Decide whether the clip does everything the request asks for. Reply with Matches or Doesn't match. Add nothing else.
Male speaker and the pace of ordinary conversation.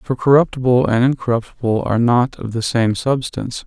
Matches